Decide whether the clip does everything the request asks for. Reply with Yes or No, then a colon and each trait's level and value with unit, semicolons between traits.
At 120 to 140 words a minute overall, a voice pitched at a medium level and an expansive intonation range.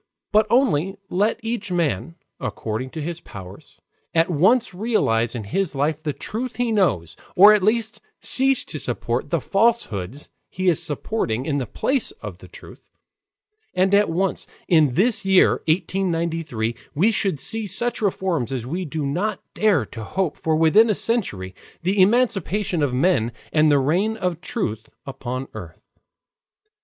No: average, 155 wpm; medium, 175 Hz; wide, 7.1 semitones